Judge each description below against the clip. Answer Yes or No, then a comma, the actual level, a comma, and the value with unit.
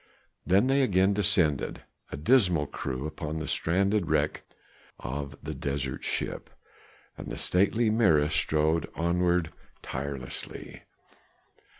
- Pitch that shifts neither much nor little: Yes, average, 4.9 semitones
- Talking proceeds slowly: Yes, slow, 110 wpm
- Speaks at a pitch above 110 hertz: No, very low, 80 Hz